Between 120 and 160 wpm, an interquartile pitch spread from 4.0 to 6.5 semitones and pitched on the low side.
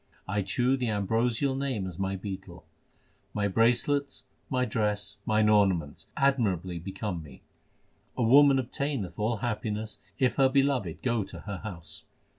Yes: average, 140 wpm; average, 4.8 semitones; low, 105 Hz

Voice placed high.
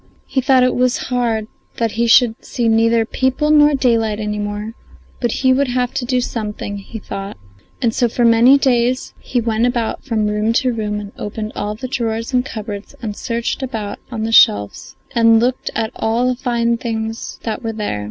Yes: high, 230 Hz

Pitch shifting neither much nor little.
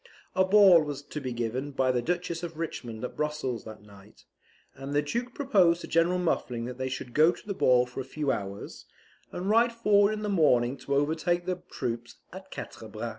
No: wide, 6.2 semitones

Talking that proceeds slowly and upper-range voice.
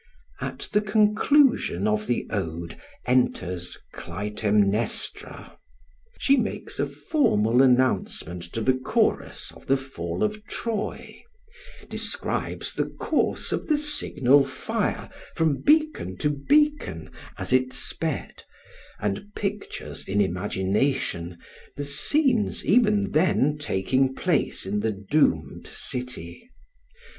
No: slow, 110 wpm; low, 130 Hz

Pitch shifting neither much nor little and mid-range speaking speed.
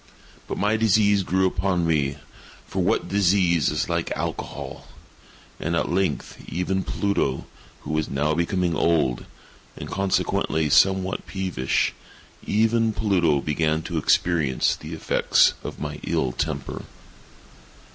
No: average, 4.0 semitones; slow, 115 wpm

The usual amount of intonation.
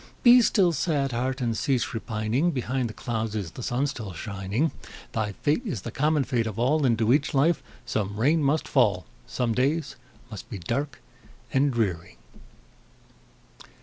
Yes: average, 4.8 semitones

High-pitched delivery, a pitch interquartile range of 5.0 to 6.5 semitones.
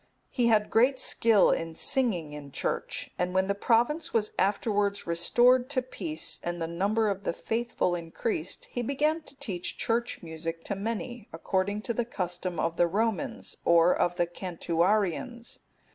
Yes: high, 200 Hz; average, 5.3 semitones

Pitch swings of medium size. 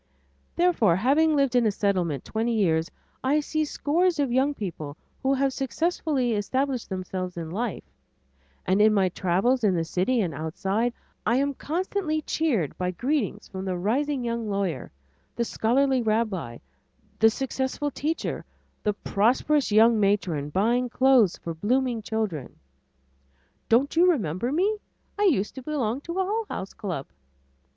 No: wide, 6.5 semitones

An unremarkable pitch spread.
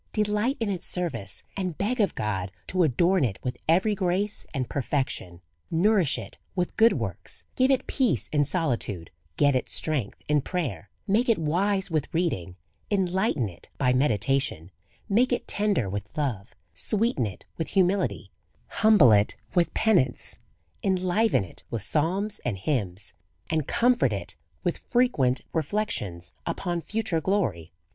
No: wide, 8.8 semitones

